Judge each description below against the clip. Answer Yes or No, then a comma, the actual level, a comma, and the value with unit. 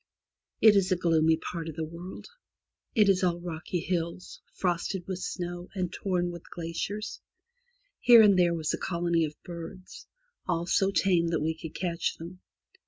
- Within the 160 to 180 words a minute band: Yes, average, 170 wpm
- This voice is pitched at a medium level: Yes, medium, 175 Hz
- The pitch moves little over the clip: Yes, narrow, 1.8 semitones